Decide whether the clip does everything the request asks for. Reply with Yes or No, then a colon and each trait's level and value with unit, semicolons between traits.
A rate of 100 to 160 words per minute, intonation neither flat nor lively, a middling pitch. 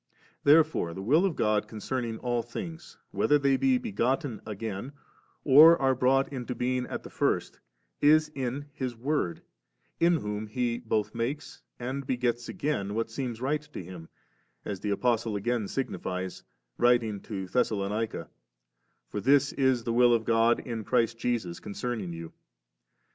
No: average, 155 wpm; average, 4.0 semitones; low, 120 Hz